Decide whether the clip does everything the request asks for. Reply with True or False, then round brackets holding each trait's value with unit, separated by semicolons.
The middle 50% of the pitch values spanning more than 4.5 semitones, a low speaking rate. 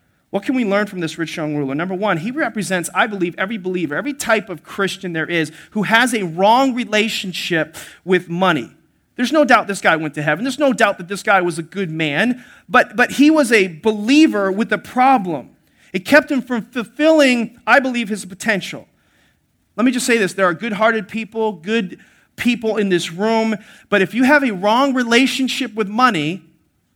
False (5.2 semitones; 200 wpm)